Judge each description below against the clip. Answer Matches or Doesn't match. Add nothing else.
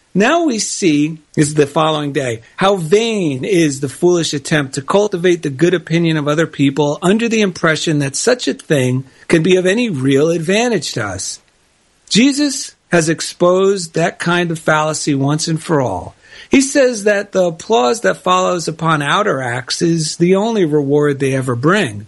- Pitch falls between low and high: Matches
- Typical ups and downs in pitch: Matches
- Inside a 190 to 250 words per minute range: Doesn't match